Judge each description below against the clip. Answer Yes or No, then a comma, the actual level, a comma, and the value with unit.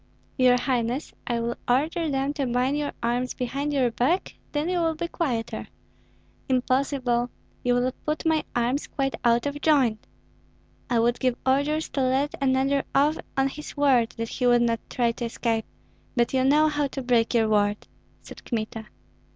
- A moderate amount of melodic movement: Yes, average, 3.2 semitones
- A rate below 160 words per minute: No, average, 175 wpm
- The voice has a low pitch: No, very high, 255 Hz